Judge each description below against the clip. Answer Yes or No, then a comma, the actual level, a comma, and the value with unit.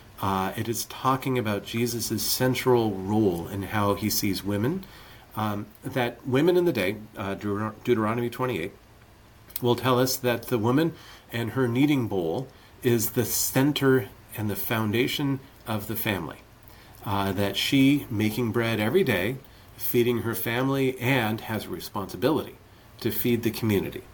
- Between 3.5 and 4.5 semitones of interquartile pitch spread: No, average, 3.1 semitones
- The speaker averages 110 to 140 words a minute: No, average, 150 wpm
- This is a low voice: Yes, low, 115 Hz